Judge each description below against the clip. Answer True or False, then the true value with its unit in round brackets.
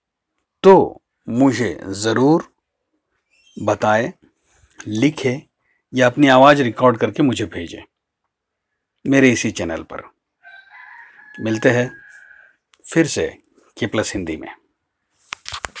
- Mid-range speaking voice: False (130 Hz)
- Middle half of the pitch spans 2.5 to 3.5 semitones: False (4.2 semitones)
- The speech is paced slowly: True (90 wpm)